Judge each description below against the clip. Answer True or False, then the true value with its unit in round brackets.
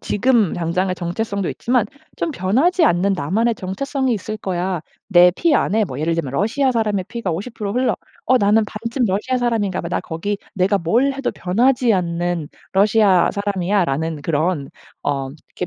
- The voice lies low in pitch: False (200 Hz)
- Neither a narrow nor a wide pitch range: True (4.8 semitones)